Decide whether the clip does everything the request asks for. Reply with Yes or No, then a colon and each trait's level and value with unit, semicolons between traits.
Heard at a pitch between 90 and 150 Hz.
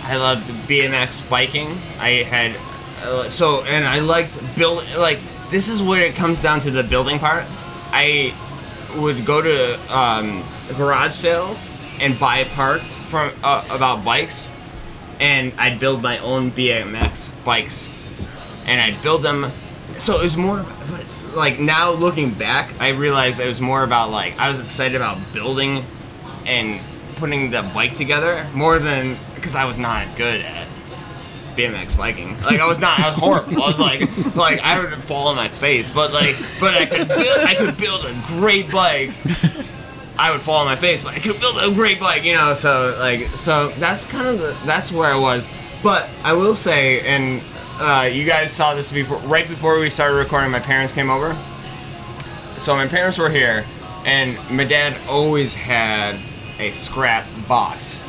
Yes: medium, 140 Hz